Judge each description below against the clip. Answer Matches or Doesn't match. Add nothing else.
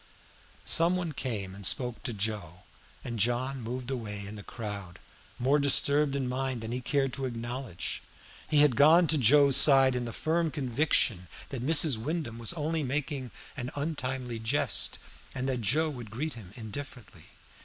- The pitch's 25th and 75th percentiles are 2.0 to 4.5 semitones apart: Matches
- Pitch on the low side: Matches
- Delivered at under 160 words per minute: Doesn't match